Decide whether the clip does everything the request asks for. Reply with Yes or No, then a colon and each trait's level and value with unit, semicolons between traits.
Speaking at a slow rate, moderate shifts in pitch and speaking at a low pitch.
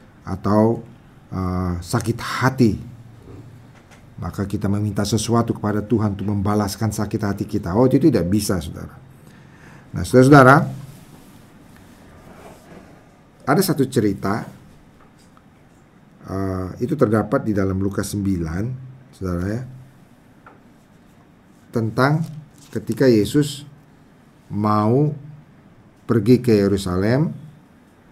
Yes: slow, 85 wpm; average, 4.2 semitones; low, 110 Hz